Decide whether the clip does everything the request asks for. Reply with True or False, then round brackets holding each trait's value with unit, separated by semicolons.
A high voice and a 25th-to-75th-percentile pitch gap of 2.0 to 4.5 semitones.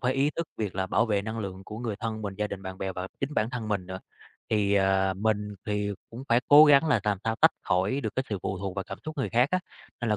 False (105 Hz; 3.8 semitones)